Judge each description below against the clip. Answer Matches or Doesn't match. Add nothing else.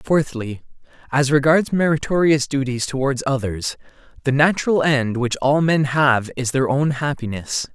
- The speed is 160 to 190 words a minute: Doesn't match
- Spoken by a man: Matches